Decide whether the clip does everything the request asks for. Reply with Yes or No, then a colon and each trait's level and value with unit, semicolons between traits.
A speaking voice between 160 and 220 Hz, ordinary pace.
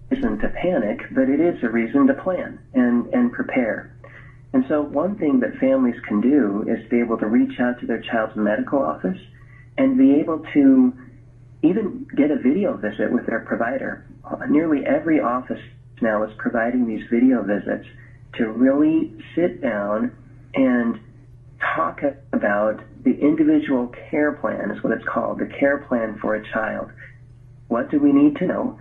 No: low, 130 Hz; average, 165 wpm